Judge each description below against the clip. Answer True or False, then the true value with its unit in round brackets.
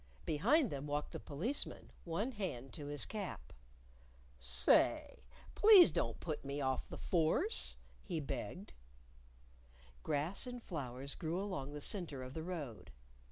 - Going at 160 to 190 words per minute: False (135 wpm)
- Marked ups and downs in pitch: True (6.3 semitones)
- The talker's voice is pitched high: False (155 Hz)